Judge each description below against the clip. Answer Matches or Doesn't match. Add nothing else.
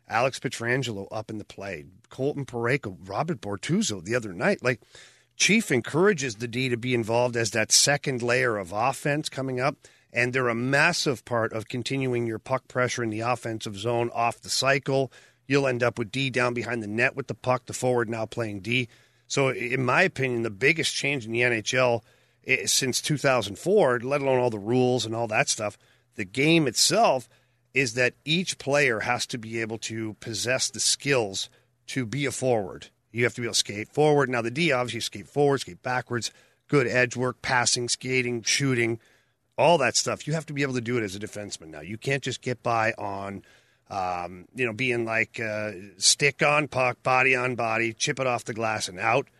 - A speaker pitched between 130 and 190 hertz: Doesn't match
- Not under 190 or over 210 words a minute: Matches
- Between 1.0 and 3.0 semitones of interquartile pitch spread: Matches